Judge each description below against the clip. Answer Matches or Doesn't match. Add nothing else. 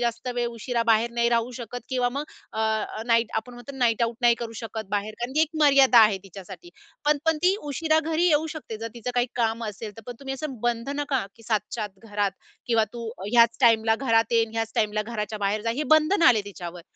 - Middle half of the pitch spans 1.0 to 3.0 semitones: Matches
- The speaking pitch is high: Matches